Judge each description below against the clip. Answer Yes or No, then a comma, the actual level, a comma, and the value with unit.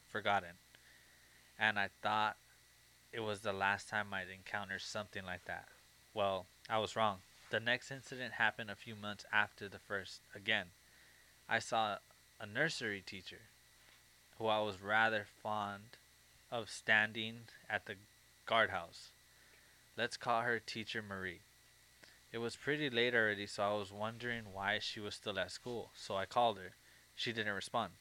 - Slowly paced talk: No, average, 150 wpm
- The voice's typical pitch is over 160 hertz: No, low, 105 Hz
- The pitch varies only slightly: Yes, narrow, 2.1 semitones